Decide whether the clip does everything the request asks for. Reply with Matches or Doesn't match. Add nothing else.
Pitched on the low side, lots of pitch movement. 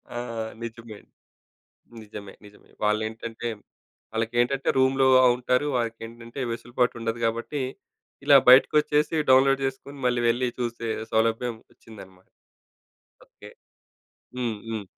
Doesn't match